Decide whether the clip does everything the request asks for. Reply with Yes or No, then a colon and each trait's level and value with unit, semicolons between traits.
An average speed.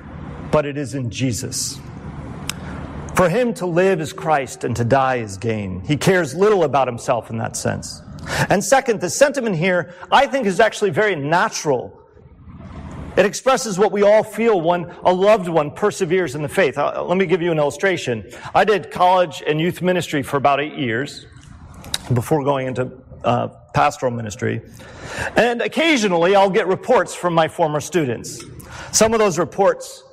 Yes: average, 165 wpm